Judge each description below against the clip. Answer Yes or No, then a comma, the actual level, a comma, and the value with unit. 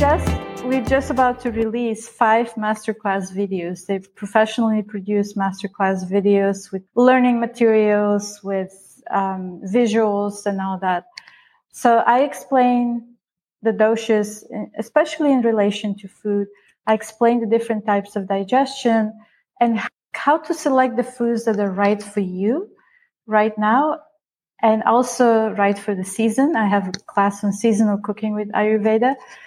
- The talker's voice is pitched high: Yes, high, 220 Hz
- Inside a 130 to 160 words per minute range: Yes, average, 140 wpm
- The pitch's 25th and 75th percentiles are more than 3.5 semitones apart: No, average, 2.9 semitones